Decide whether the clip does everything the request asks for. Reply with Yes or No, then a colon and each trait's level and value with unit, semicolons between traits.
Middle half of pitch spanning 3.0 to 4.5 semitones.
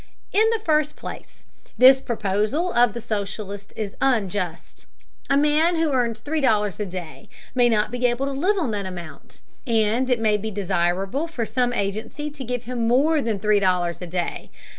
No: average, 5.2 semitones